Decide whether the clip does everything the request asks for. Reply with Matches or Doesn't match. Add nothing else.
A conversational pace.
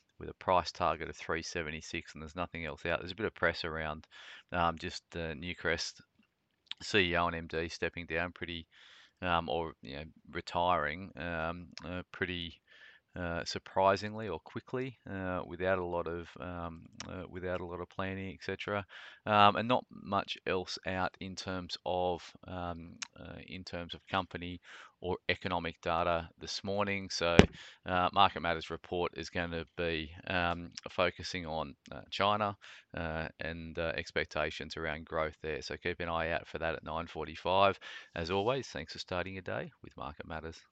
Matches